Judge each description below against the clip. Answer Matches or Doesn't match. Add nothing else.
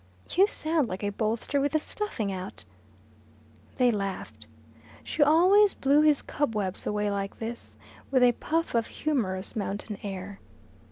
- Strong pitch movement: Matches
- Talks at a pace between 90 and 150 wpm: Matches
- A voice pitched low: Doesn't match